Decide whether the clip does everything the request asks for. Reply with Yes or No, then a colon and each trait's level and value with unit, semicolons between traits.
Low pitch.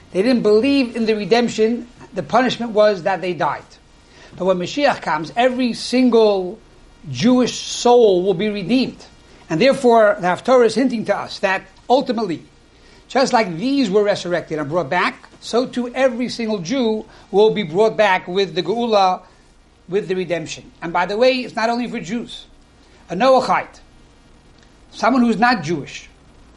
No: high, 220 Hz